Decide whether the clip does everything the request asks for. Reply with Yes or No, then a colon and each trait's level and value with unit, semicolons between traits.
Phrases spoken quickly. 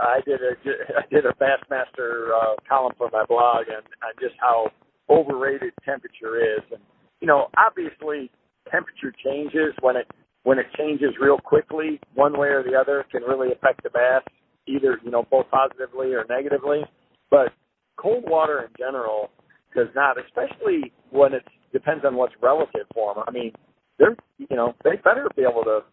No: average, 175 wpm